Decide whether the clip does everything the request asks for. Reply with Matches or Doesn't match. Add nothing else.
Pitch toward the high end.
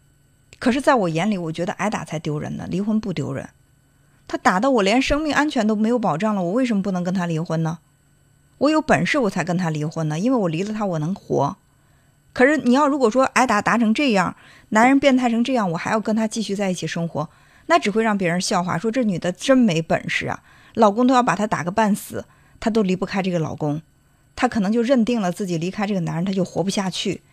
Matches